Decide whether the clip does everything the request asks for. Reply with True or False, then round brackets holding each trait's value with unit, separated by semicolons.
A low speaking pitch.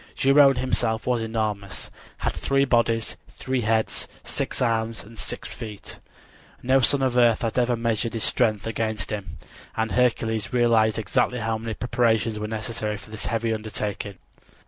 True (115 Hz)